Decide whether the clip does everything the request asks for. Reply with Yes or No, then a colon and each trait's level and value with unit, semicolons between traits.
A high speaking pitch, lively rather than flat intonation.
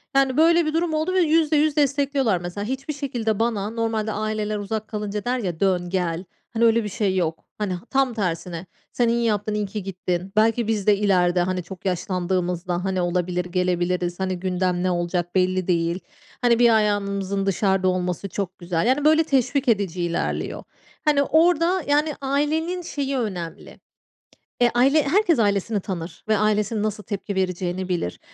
Yes: high, 205 Hz; wide, 5.8 semitones